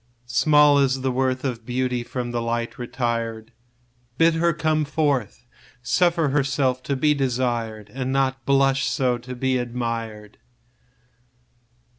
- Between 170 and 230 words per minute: No, slow, 135 wpm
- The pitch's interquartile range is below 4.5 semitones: Yes, narrow, 2.5 semitones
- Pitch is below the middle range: Yes, low, 130 Hz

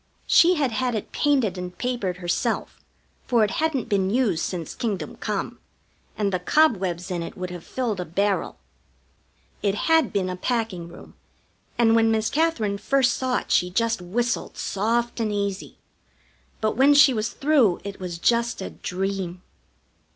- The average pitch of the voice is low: No, high, 215 Hz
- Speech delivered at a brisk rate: No, average, 165 wpm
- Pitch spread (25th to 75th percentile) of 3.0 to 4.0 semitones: No, average, 4.9 semitones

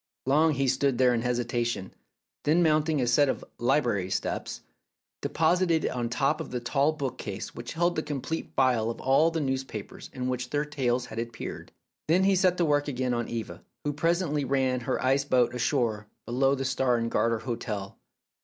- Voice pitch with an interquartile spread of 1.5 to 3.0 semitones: No, average, 3.8 semitones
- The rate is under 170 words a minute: No, average, 190 wpm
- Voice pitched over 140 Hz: No, low, 130 Hz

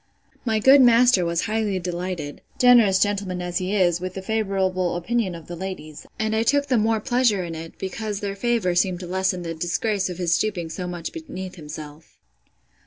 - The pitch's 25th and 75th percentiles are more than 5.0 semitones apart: No, average, 3.9 semitones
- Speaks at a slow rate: No, average, 190 wpm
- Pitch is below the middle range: No, high, 190 Hz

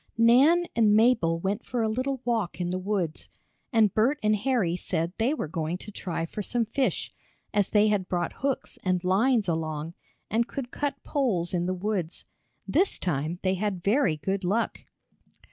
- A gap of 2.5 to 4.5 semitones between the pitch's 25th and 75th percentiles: No, average, 5.0 semitones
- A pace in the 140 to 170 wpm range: No, average, 180 wpm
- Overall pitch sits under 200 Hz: No, high, 205 Hz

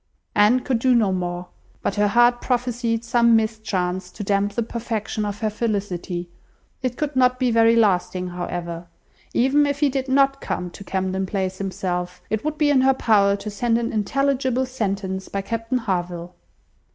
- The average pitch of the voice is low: No, high, 220 Hz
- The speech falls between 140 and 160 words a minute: No, average, 175 wpm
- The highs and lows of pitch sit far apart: No, average, 4.7 semitones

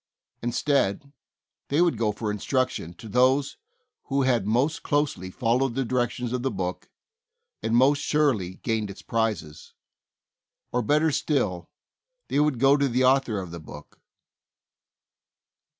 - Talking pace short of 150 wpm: Yes, average, 140 wpm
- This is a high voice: No, low, 125 Hz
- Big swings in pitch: No, average, 4.6 semitones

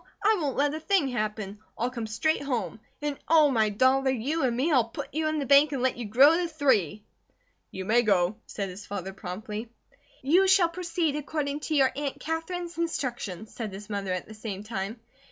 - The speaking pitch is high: Yes, very high, 260 Hz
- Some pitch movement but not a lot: No, wide, 6.4 semitones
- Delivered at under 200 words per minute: No, fast, 205 wpm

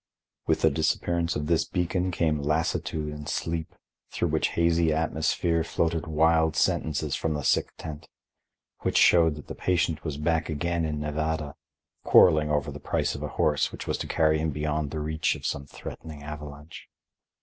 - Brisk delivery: No, average, 170 wpm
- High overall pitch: No, very low, 80 Hz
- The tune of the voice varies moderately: No, narrow, 1.6 semitones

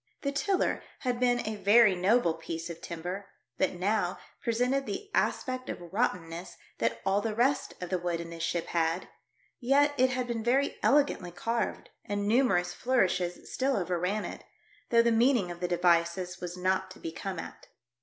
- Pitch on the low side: No, high, 195 Hz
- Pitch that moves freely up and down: Yes, wide, 5.7 semitones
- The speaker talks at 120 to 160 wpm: No, average, 175 wpm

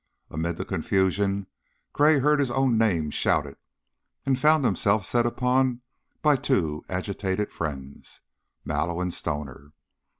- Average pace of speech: No, slow, 125 wpm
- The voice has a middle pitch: No, low, 100 Hz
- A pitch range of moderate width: No, wide, 7.5 semitones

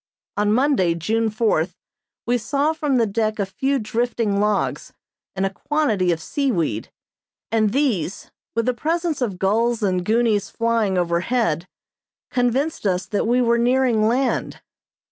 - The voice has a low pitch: No, high, 225 Hz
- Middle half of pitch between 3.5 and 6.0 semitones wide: Yes, average, 4.1 semitones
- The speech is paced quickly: No, average, 145 wpm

